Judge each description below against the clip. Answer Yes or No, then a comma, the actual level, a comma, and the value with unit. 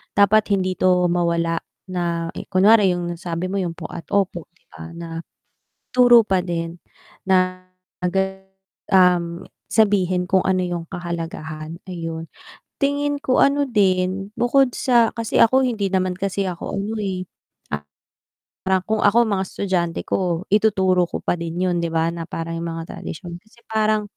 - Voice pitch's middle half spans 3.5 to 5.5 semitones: No, average, 3.0 semitones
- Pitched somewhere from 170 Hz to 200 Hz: Yes, medium, 185 Hz